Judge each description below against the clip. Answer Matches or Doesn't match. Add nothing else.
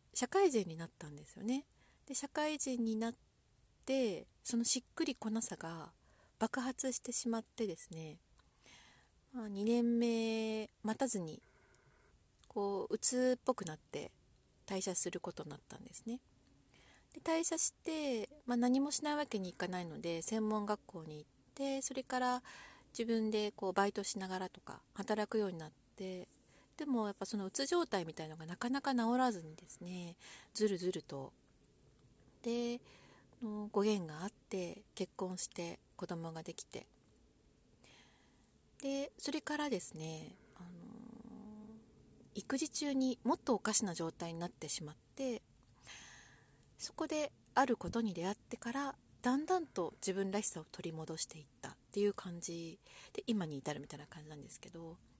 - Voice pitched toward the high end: Matches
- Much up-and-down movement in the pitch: Matches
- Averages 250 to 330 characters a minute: Matches